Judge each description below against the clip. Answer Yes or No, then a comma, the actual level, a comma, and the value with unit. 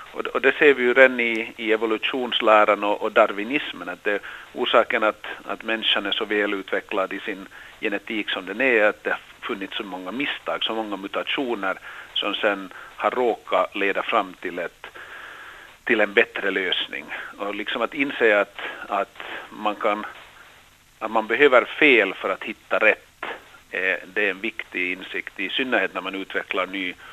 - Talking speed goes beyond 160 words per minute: Yes, average, 170 wpm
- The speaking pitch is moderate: No, low, 110 Hz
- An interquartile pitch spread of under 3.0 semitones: Yes, narrow, 2.4 semitones